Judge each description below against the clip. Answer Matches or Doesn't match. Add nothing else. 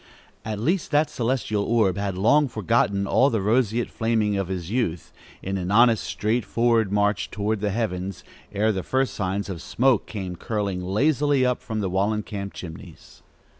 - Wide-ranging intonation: Doesn't match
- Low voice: Matches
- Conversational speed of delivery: Matches